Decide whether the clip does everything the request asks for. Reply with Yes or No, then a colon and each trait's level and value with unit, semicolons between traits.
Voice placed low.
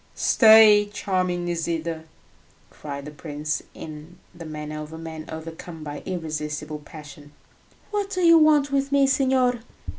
No: medium, 165 Hz